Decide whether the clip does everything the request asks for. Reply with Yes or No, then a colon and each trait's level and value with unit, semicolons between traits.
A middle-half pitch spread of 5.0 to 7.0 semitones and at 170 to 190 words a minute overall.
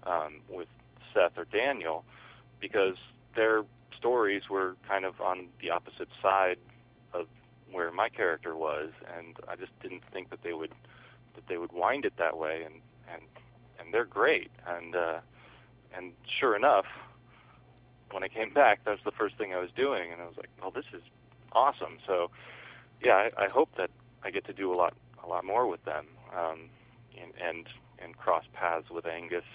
No: average, 4.3 semitones; average, 185 wpm